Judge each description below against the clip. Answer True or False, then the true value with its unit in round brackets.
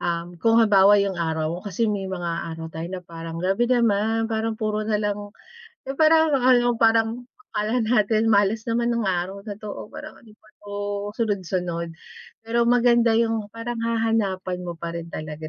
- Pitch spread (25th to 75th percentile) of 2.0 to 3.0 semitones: False (4.1 semitones)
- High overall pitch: True (210 Hz)